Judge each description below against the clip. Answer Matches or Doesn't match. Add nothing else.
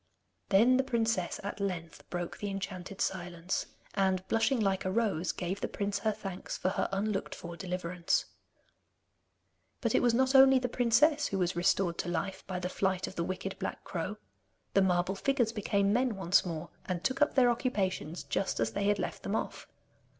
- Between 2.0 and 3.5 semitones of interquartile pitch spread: Doesn't match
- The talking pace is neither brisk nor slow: Matches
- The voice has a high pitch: Matches